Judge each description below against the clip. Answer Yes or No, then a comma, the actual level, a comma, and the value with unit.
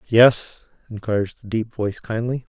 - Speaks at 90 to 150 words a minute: Yes, average, 140 wpm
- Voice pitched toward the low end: Yes, low, 110 Hz